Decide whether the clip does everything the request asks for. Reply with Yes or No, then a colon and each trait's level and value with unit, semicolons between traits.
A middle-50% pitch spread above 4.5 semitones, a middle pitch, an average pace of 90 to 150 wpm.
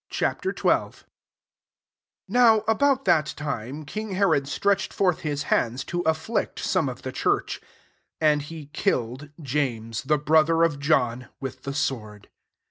Yes: average, 4.9 semitones; medium, 150 Hz; average, 140 wpm